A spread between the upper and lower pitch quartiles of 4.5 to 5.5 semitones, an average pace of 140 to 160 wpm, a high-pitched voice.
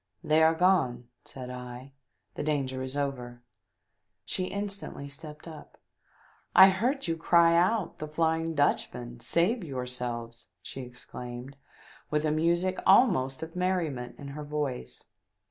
No: average, 5.2 semitones; average, 145 wpm; medium, 150 Hz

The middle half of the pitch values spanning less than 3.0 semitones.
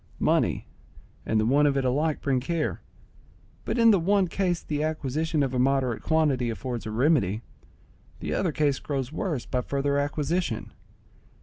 No: average, 3.8 semitones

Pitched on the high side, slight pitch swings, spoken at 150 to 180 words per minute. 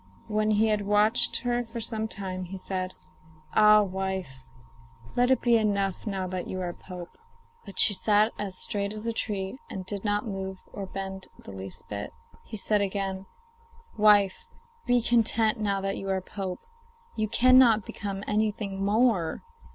Yes: high, 205 Hz; narrow, 2.2 semitones; average, 165 wpm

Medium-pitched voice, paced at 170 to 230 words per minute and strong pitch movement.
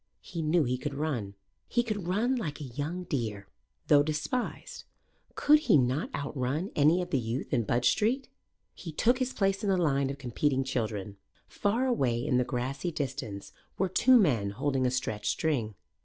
Yes: medium, 145 Hz; average, 180 wpm; wide, 6.6 semitones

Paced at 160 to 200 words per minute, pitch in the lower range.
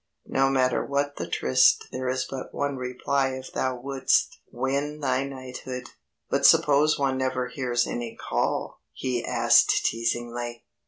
No: average, 145 wpm; low, 130 Hz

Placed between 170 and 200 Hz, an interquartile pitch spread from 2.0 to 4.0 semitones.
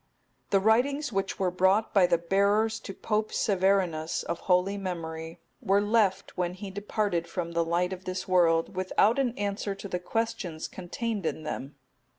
Yes: high, 190 Hz; average, 3.0 semitones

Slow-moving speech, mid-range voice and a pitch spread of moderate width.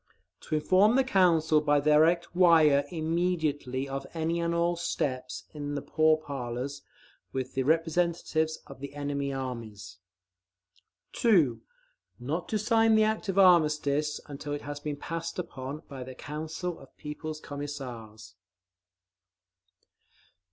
Yes: slow, 125 wpm; medium, 150 Hz; average, 3.3 semitones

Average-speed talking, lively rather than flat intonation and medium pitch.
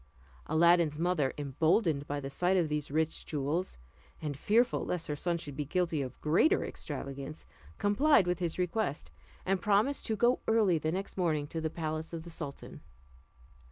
No: average, 175 wpm; average, 3.6 semitones; medium, 165 Hz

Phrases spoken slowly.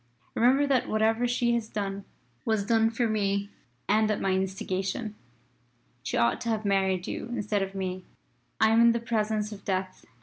No: average, 175 wpm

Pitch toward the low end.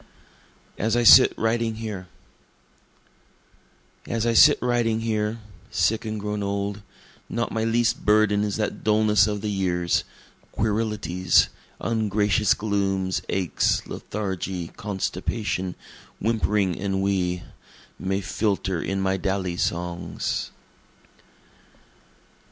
Yes: low, 105 Hz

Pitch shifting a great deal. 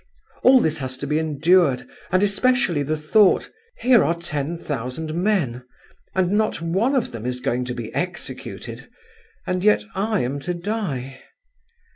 Yes: wide, 6.4 semitones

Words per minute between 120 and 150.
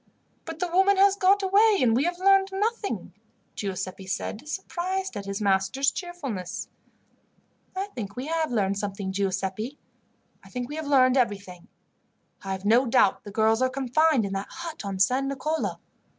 No: average, 165 wpm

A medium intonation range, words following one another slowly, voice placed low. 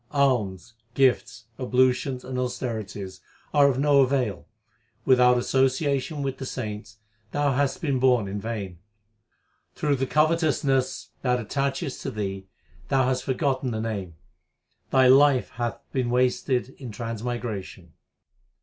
Yes: average, 3.3 semitones; slow, 125 wpm; low, 125 Hz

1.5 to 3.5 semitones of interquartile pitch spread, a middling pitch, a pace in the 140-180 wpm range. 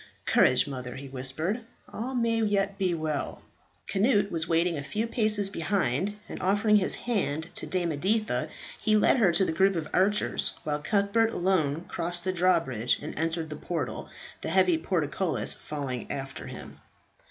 No: average, 4.9 semitones; medium, 180 Hz; average, 165 wpm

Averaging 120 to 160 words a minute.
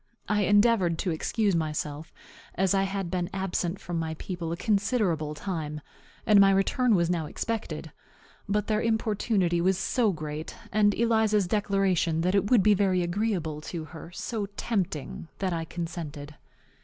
Yes: average, 155 wpm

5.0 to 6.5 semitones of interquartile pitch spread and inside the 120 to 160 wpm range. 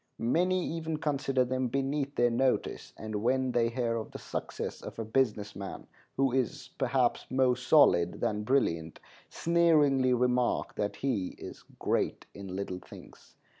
No: average, 3.7 semitones; average, 150 wpm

